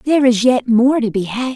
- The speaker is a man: No, female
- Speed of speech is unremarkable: No, fast, 270 wpm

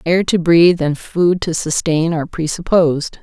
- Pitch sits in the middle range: Yes, medium, 165 Hz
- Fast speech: No, average, 165 wpm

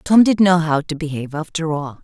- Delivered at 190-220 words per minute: No, fast, 235 wpm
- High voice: No, medium, 160 Hz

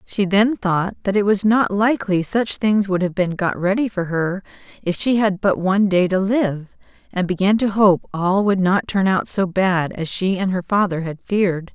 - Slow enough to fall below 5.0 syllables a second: Yes, 4.7 syllables/s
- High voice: Yes, high, 195 Hz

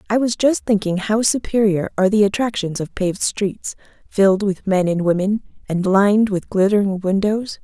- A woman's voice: Yes, female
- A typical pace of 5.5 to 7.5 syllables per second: No, 5.1 syllables/s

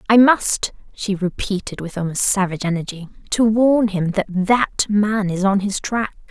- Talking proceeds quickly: No, average, 170 wpm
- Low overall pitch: No, high, 200 Hz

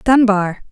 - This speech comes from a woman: Yes, female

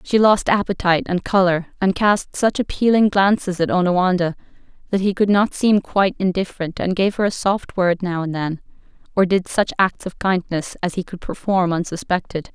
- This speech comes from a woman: Yes, female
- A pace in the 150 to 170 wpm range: No, average, 185 wpm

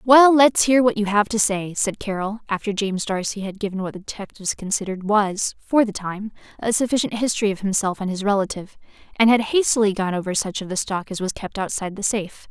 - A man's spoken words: No, female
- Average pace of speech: No, fast, 220 wpm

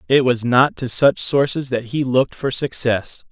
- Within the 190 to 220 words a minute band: Yes, average, 200 wpm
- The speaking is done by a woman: No, male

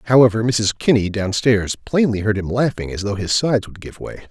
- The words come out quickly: Yes, fast, 225 wpm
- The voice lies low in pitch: Yes, low, 110 Hz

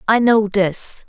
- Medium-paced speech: Yes, average, 165 wpm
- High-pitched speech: Yes, high, 210 Hz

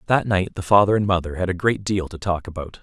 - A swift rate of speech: Yes, fast, 275 wpm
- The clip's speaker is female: No, male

